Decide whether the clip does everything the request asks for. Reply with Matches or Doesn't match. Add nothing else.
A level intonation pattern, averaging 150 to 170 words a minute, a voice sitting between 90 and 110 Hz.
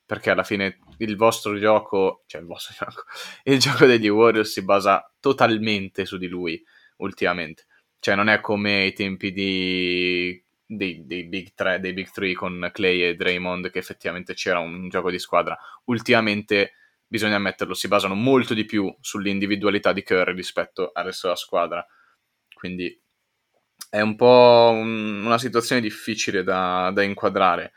Doesn't match